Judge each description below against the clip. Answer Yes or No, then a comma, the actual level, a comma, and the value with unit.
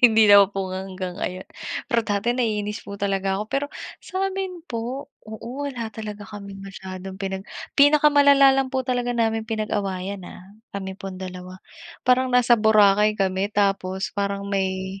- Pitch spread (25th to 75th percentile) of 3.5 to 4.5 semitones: Yes, average, 4.0 semitones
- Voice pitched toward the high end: Yes, high, 205 Hz